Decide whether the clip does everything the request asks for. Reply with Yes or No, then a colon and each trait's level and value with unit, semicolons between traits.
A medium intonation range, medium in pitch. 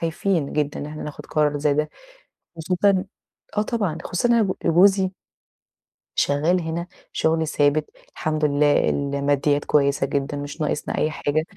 Yes: average, 3.3 semitones; medium, 155 Hz